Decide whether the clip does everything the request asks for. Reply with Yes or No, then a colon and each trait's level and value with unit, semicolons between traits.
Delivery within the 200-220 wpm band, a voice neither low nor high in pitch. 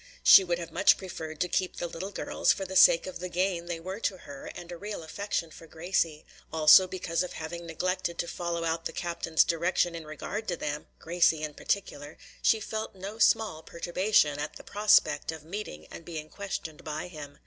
Yes: fast, 205 wpm; medium, 170 Hz